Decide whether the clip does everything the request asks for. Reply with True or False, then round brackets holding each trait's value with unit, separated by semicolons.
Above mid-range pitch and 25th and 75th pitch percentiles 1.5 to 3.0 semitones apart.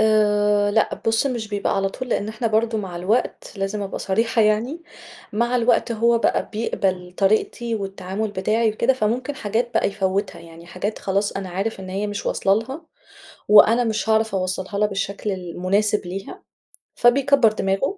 True (210 Hz; 2.7 semitones)